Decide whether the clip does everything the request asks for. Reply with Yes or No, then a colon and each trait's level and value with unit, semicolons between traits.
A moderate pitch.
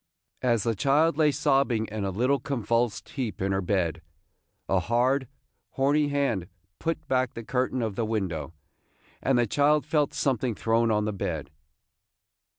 No: low, 120 Hz